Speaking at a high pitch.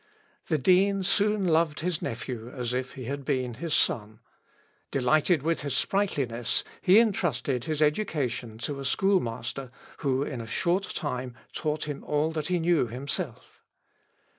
No: medium, 145 Hz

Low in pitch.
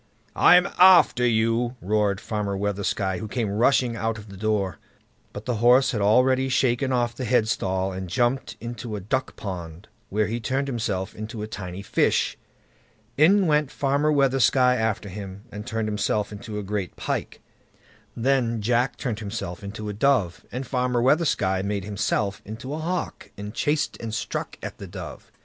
Yes: low, 110 Hz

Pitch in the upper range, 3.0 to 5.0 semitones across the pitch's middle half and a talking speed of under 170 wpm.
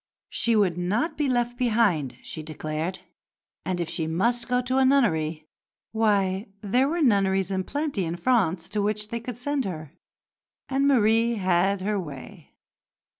No: high, 205 Hz; wide, 5.6 semitones; average, 160 wpm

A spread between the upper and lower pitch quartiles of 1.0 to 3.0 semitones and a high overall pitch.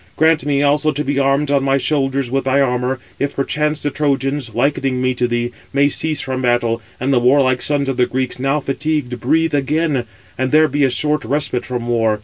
No: narrow, 2.6 semitones; low, 135 Hz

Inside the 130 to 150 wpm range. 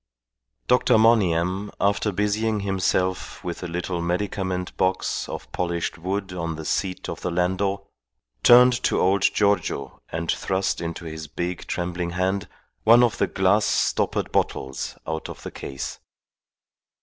Yes: average, 140 wpm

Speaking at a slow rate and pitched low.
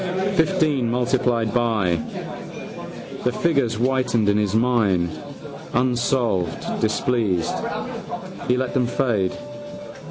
Yes: slow, 90 wpm; low, 120 Hz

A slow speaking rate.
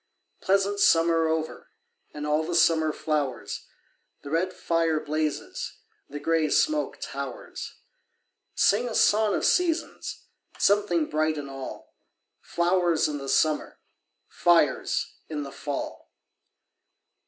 Yes: slow, 115 wpm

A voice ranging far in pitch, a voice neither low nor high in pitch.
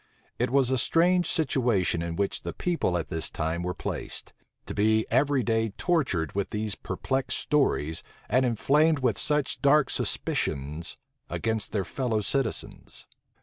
No: wide, 6.7 semitones; low, 115 Hz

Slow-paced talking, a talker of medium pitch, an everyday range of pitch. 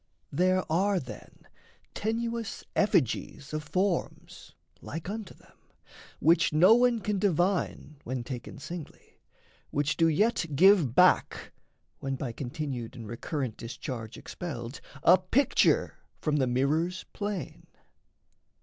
No: slow, 115 wpm; medium, 165 Hz; wide, 6.3 semitones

